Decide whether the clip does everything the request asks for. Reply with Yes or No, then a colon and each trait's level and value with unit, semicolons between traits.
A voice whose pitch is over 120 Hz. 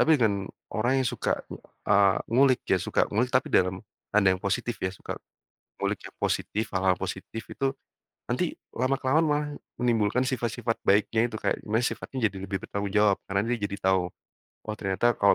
No: low, 110 Hz